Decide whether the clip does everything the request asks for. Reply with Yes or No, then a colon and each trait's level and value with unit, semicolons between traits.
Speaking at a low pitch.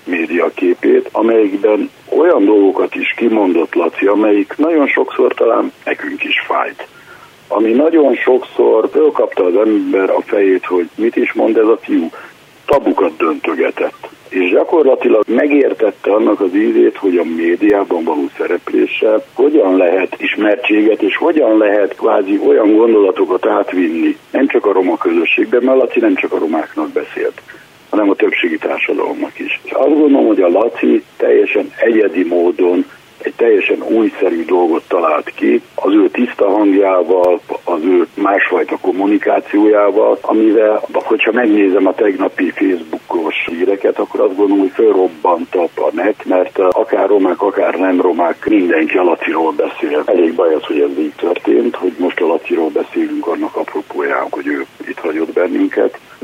No: very high, 360 Hz